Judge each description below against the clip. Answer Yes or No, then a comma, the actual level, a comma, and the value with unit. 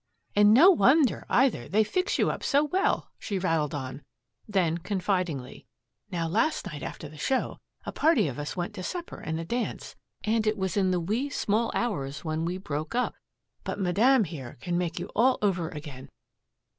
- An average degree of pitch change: No, wide, 6.6 semitones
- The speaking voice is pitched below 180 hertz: No, medium, 185 Hz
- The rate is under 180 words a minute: No, average, 185 wpm